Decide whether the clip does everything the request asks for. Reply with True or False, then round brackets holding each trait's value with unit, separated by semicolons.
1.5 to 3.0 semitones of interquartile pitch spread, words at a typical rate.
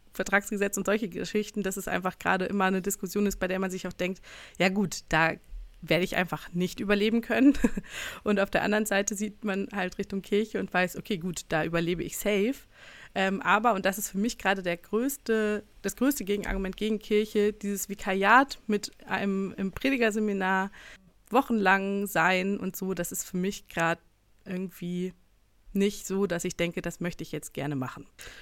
True (2.4 semitones; 180 wpm)